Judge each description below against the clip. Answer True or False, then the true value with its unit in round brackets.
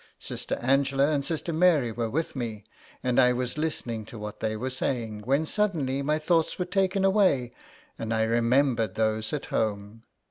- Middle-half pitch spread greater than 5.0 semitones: True (5.5 semitones)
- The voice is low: True (130 Hz)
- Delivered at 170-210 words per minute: True (175 wpm)